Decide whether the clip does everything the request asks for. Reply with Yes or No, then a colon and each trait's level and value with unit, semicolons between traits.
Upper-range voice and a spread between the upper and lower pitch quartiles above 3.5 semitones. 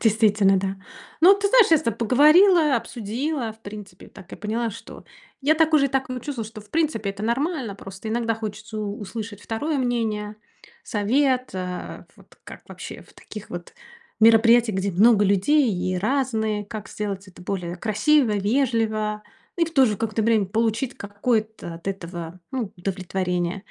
Yes: high, 220 Hz; average, 4.1 semitones